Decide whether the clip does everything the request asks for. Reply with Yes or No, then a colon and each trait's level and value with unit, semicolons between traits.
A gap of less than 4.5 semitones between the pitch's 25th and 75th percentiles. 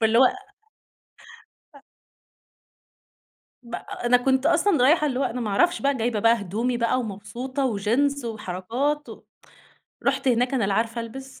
Yes: average, 3.2 semitones